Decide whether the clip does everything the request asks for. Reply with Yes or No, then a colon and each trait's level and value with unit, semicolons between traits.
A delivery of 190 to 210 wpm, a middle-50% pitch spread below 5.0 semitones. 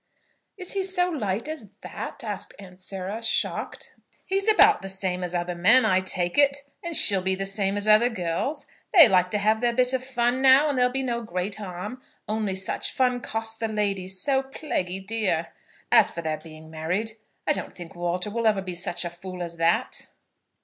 No: average, 200 wpm; wide, 5.5 semitones